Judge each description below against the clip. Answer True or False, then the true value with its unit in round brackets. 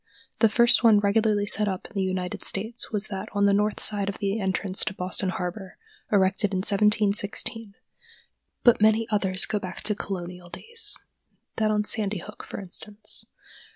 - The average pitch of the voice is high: True (205 Hz)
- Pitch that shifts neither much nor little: False (2.0 semitones)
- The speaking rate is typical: True (165 wpm)